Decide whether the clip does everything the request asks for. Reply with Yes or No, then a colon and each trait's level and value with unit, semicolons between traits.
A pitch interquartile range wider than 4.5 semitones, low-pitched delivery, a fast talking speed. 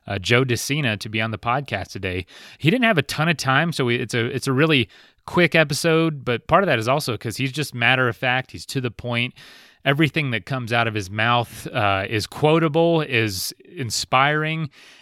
Yes: average, 5.1 semitones; low, 130 Hz; fast, 210 wpm